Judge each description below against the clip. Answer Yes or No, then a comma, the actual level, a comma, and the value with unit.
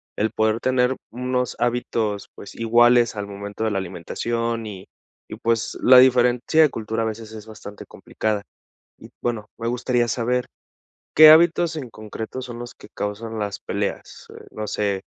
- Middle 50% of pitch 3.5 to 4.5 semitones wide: No, narrow, 2.5 semitones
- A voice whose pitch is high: No, low, 115 Hz